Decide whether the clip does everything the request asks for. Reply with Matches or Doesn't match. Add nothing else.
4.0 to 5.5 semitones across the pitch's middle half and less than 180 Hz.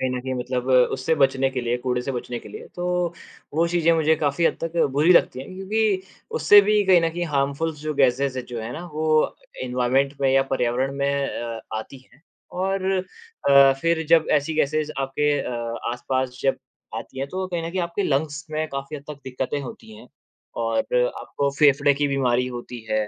Matches